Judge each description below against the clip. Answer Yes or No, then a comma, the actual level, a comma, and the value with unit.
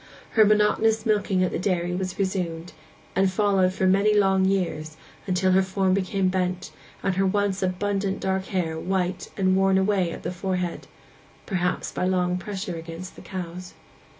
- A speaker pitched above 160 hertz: Yes, high, 190 Hz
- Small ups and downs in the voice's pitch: Yes, narrow, 1.4 semitones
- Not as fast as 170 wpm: Yes, average, 160 wpm